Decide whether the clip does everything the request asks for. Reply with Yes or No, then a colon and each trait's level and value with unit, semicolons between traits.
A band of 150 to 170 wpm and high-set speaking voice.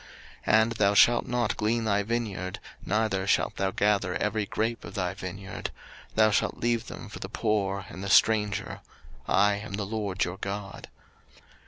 No: average, 165 wpm; low, 105 Hz